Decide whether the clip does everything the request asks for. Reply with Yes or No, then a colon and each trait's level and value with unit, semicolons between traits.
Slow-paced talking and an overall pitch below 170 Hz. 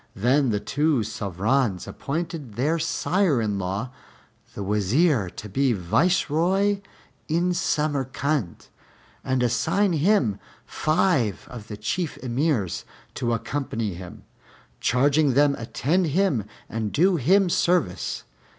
Yes: slow, 115 wpm; low, 135 Hz